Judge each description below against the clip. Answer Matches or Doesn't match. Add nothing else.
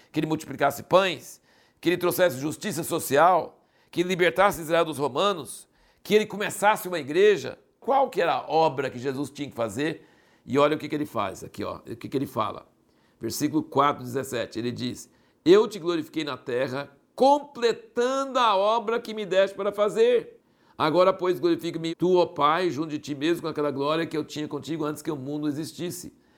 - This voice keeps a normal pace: Doesn't match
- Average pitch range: Doesn't match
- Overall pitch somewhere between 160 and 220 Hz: Matches